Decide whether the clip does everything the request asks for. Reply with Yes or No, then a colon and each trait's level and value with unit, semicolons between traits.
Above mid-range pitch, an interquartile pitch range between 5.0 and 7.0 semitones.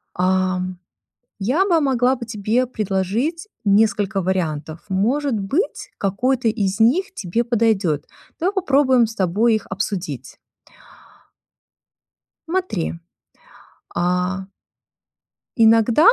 Yes: high, 220 Hz; wide, 5.6 semitones